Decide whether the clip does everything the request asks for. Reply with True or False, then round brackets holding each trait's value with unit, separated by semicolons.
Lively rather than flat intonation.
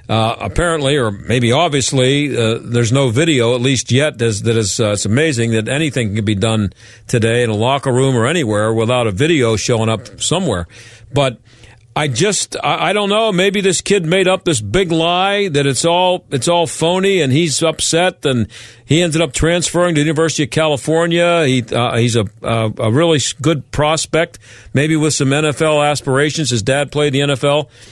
True (5.8 semitones)